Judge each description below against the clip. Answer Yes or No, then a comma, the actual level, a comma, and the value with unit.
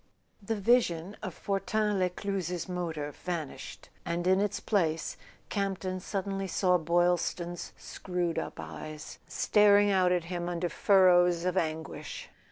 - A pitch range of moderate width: No, narrow, 2.3 semitones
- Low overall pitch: No, medium, 180 Hz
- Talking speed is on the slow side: Yes, slow, 125 wpm